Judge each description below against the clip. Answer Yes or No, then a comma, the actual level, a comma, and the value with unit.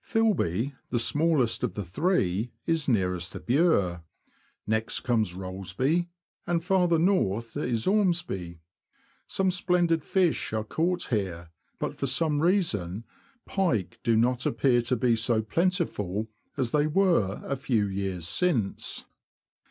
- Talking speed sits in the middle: No, slow, 130 wpm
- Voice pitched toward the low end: Yes, low, 125 Hz